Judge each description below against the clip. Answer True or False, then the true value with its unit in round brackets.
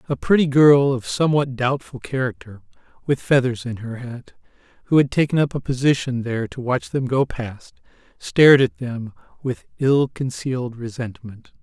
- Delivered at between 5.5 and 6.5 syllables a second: False (4.9 syllables/s)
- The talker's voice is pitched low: True (130 Hz)